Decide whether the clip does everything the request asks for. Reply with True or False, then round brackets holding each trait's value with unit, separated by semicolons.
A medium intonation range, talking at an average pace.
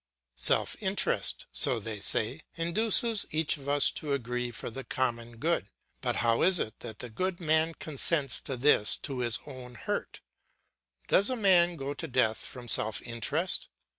False (5.8 semitones; 165 wpm)